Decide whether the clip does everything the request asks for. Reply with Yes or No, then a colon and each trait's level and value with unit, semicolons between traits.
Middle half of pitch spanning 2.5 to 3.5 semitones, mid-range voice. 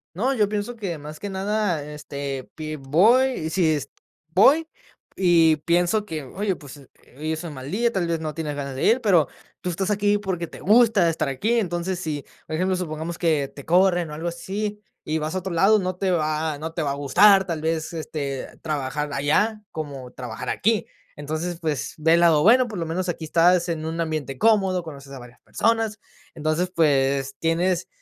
No: average, 4.0 semitones; medium, 165 Hz